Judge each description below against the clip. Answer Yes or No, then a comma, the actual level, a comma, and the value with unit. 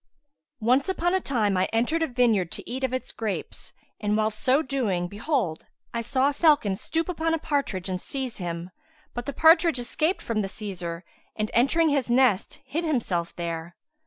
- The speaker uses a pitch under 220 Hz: No, high, 240 Hz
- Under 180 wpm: No, average, 190 wpm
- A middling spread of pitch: No, wide, 6.7 semitones